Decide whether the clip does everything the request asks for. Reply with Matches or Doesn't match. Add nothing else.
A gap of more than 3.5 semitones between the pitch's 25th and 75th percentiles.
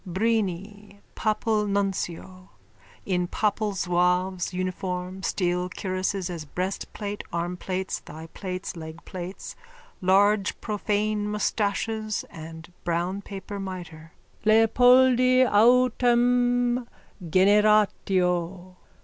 Doesn't match